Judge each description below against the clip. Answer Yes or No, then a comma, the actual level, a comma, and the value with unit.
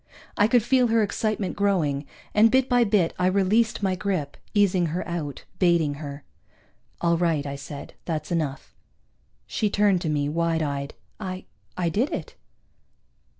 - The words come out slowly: No, average, 155 wpm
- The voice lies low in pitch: No, medium, 180 Hz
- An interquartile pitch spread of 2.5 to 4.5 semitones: No, average, 5.1 semitones